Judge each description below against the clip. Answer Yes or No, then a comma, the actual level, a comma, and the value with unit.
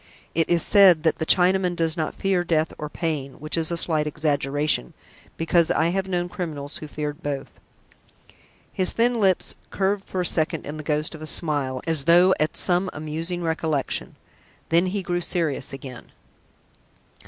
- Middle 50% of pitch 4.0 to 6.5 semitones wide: No, average, 2.8 semitones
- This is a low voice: No, medium, 165 Hz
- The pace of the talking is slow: No, average, 170 wpm